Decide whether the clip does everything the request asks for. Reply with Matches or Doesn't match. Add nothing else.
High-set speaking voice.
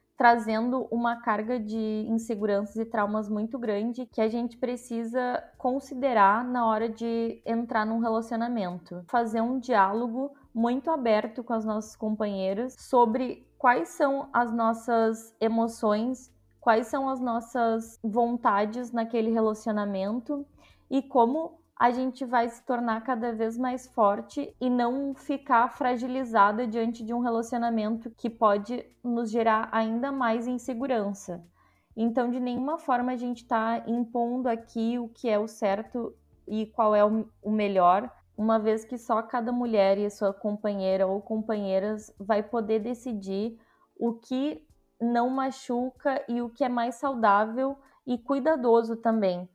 Matches